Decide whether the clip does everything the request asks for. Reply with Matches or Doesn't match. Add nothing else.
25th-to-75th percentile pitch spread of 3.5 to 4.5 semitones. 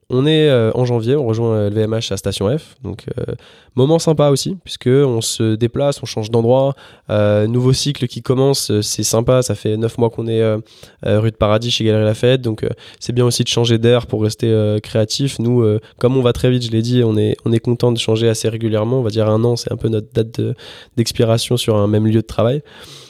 Doesn't match